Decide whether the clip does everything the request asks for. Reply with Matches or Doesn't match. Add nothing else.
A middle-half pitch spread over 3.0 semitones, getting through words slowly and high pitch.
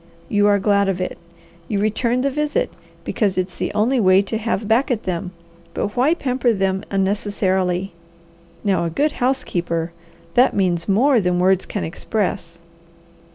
Doesn't match